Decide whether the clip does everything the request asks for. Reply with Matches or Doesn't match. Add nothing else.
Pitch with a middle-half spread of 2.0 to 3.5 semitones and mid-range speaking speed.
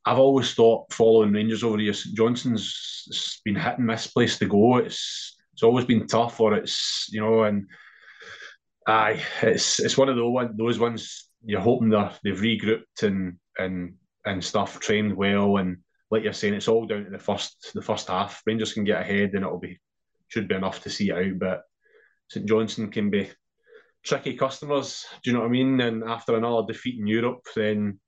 Matches